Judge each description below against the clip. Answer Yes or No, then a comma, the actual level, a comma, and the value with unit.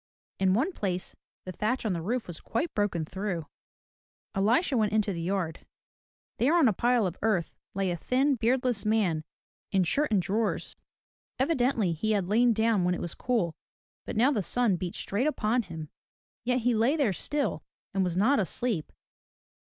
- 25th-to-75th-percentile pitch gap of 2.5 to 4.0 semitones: No, average, 5.1 semitones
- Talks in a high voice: Yes, high, 215 Hz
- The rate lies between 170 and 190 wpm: Yes, average, 175 wpm